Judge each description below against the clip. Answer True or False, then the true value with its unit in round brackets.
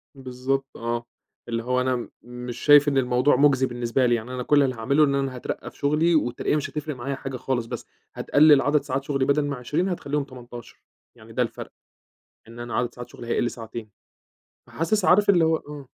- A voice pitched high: False (130 Hz)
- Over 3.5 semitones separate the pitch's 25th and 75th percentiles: False (3.1 semitones)